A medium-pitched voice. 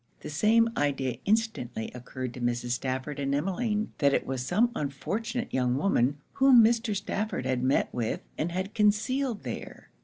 Yes: medium, 150 Hz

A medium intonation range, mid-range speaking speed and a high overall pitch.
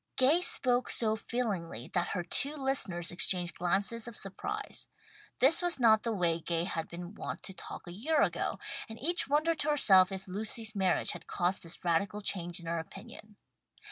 No: wide, 6.1 semitones; average, 180 wpm; high, 200 Hz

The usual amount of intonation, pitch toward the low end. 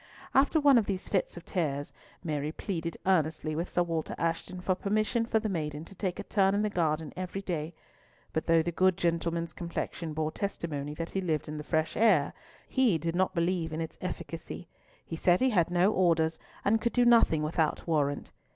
No: average, 3.3 semitones; medium, 170 Hz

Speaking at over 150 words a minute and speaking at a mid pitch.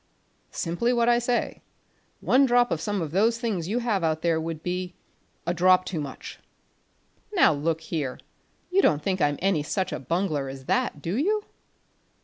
Yes: average, 175 wpm; medium, 180 Hz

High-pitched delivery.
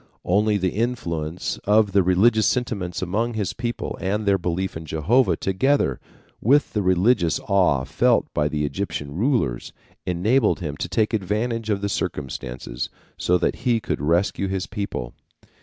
No: low, 100 Hz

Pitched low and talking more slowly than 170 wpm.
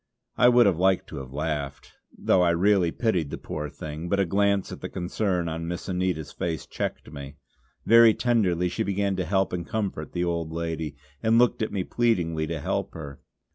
No: very low, 90 Hz; average, 200 wpm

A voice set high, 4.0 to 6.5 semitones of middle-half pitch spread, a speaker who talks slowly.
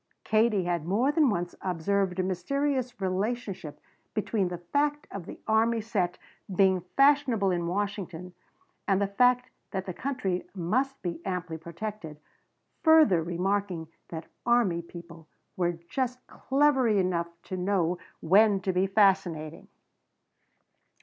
Yes: high, 195 Hz; average, 4.7 semitones; slow, 130 wpm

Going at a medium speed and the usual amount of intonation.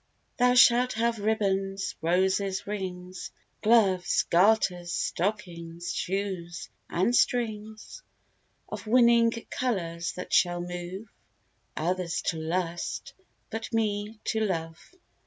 No: slow, 100 wpm; average, 4.0 semitones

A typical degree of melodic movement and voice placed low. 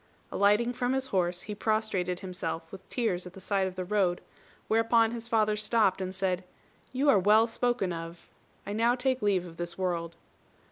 No: average, 4.0 semitones; high, 200 Hz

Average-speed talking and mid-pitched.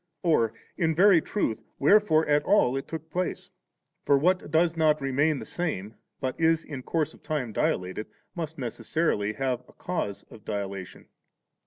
Yes: average, 165 wpm; medium, 150 Hz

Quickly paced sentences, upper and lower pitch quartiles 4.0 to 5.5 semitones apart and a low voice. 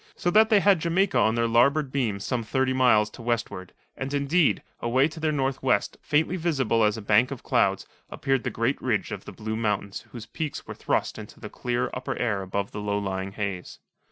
Yes: fast, 210 wpm; average, 4.8 semitones; low, 120 Hz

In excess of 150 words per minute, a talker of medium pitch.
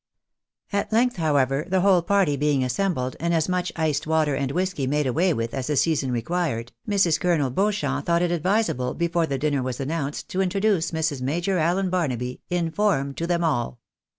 Yes: average, 190 wpm; medium, 160 Hz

